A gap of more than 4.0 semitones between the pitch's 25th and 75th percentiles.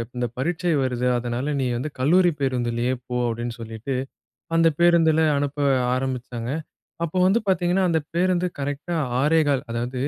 Yes: wide, 5.4 semitones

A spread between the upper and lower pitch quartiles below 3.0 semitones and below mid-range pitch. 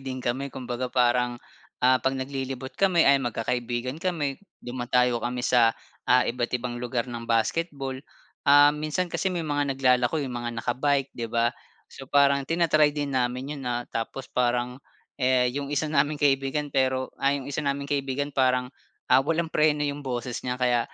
Yes: narrow, 2.6 semitones; low, 130 Hz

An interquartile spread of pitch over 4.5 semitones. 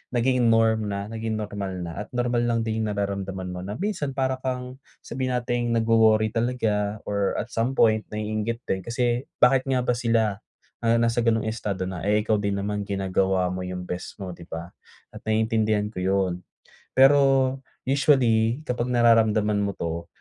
No: average, 3.2 semitones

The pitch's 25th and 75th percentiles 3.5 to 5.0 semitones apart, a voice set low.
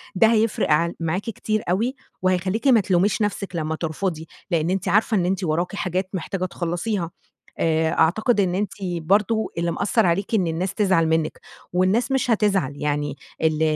No: average, 4.0 semitones; medium, 185 Hz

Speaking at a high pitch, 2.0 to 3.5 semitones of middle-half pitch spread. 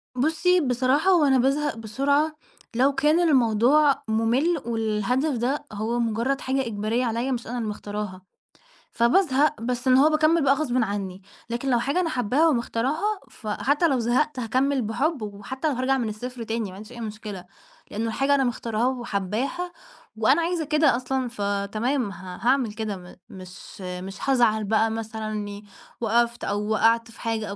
No: high, 240 Hz; average, 4.1 semitones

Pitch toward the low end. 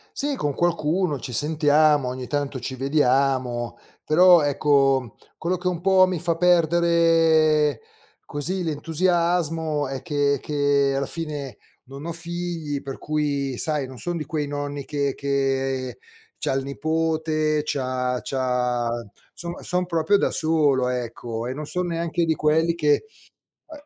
No: medium, 150 Hz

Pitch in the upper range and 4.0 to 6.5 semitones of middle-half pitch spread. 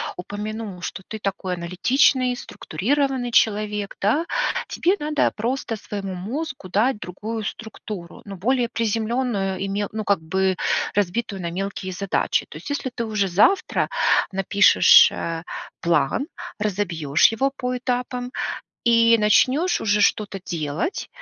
Yes: high, 210 Hz; average, 4.3 semitones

